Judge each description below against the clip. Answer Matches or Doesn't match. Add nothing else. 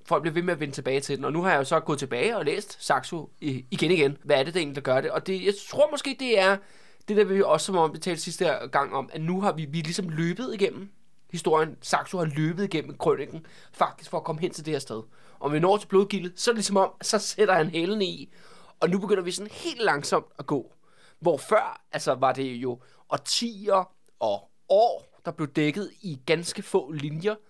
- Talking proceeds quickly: Matches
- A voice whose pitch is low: Doesn't match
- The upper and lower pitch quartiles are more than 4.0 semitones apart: Matches